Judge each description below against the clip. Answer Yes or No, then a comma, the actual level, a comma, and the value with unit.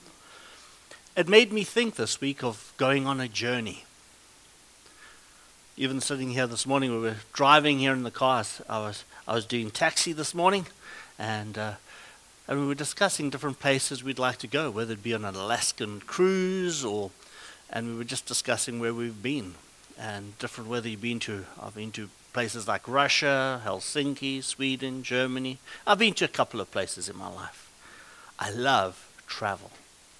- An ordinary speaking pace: Yes, average, 175 wpm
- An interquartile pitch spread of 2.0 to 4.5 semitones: Yes, average, 3.8 semitones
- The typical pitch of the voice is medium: No, low, 130 Hz